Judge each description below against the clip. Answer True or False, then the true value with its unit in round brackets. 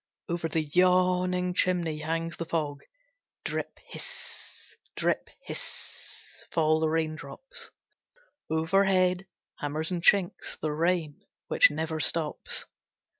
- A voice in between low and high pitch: True (165 Hz)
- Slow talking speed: True (105 wpm)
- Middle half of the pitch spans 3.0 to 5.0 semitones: False (2.5 semitones)